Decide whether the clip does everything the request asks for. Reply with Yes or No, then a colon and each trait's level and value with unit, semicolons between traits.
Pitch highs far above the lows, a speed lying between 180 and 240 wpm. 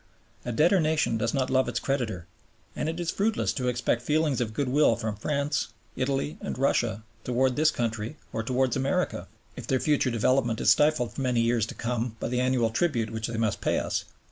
No: average, 3.6 semitones; average, 200 wpm